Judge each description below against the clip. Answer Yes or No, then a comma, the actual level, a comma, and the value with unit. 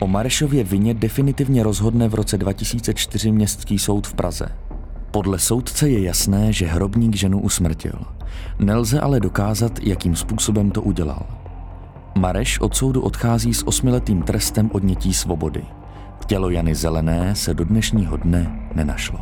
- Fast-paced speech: No, average, 135 wpm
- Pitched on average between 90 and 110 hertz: Yes, low, 100 Hz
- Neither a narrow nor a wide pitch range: Yes, average, 3.8 semitones